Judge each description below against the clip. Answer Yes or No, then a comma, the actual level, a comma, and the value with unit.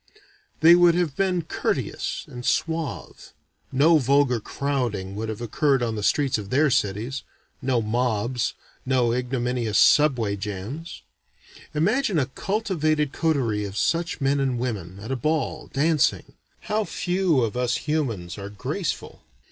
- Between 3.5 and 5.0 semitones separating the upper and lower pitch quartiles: No, wide, 5.6 semitones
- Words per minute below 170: Yes, average, 140 wpm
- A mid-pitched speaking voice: No, low, 130 Hz